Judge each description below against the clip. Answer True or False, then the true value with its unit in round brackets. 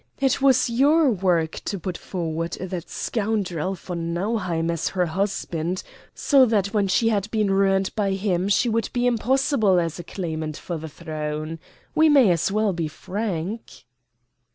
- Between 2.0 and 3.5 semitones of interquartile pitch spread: False (4.8 semitones)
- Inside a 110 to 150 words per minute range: False (160 wpm)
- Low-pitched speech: False (190 Hz)